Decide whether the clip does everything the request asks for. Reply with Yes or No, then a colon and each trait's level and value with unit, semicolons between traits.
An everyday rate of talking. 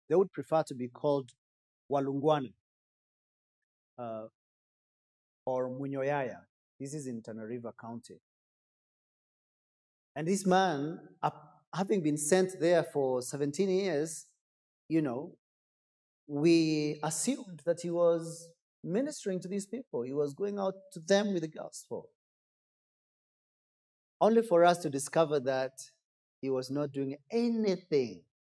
No: slow, 120 wpm